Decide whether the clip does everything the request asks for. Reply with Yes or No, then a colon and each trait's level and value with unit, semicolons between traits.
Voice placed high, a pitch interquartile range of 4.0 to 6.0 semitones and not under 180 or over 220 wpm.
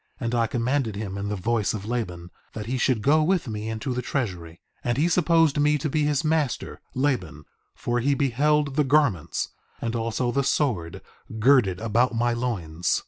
No: low, 120 Hz; average, 5.0 semitones; average, 190 wpm